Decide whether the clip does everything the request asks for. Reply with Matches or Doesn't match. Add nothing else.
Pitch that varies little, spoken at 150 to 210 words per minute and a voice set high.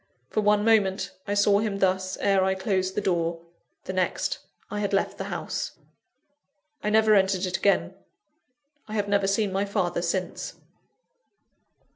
Matches